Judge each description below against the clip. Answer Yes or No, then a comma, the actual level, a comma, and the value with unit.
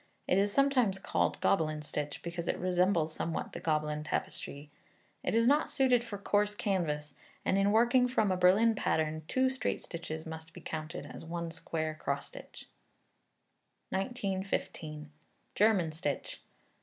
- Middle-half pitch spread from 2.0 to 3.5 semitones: No, average, 5.3 semitones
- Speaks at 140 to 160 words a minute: Yes, average, 145 wpm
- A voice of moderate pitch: Yes, medium, 180 Hz